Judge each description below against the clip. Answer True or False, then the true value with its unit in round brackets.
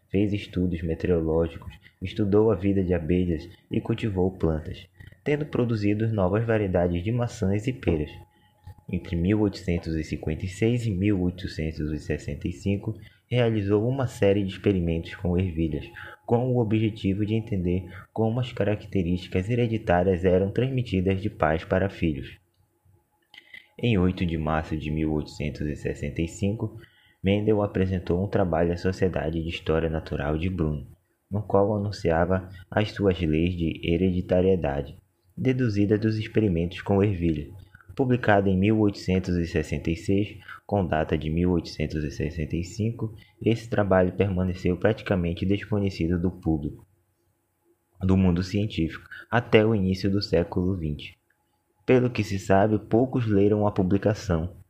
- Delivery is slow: True (115 wpm)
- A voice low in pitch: True (95 Hz)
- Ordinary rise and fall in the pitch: True (3.7 semitones)